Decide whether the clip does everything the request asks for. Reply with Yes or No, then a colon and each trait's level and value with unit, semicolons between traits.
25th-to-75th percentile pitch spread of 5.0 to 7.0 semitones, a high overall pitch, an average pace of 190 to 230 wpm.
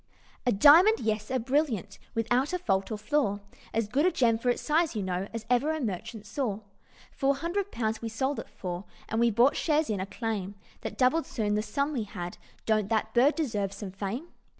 Yes: average, 5.3 semitones; high, 230 Hz; fast, 205 wpm